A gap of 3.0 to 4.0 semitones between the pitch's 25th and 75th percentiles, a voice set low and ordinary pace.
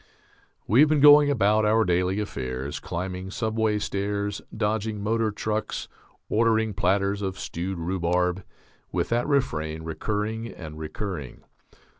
No: average, 3.6 semitones; low, 100 Hz; slow, 125 wpm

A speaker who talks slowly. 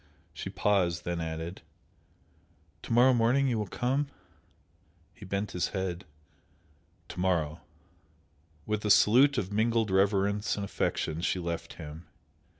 Yes: slow, 130 wpm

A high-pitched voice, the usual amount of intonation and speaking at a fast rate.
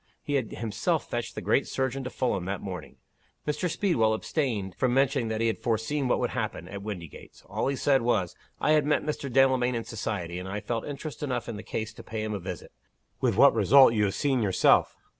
No: low, 115 Hz; average, 4.4 semitones; fast, 220 wpm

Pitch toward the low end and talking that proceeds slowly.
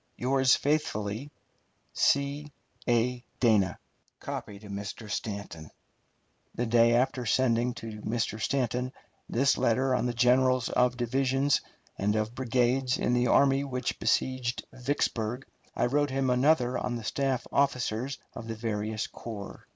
Yes: low, 125 Hz; slow, 130 wpm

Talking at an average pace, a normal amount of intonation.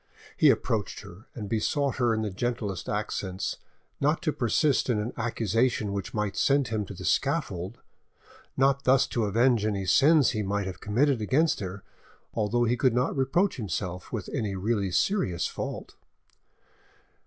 Yes: average, 160 wpm; average, 4.5 semitones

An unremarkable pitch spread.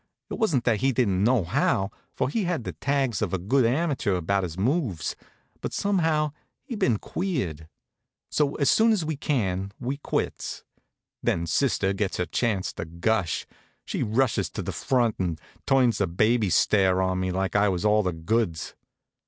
No: wide, 6.5 semitones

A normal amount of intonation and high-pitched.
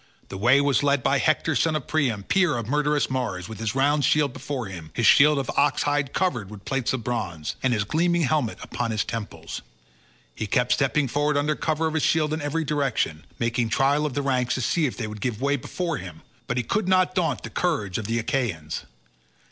No: average, 4.8 semitones; low, 135 Hz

